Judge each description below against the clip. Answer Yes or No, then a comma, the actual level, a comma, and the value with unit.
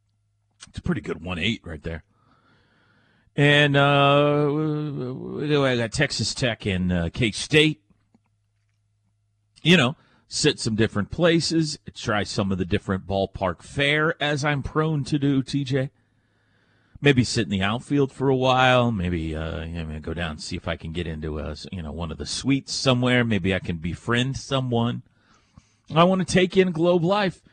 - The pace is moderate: Yes, average, 170 wpm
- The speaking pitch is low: Yes, low, 115 Hz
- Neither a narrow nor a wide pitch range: No, wide, 6.5 semitones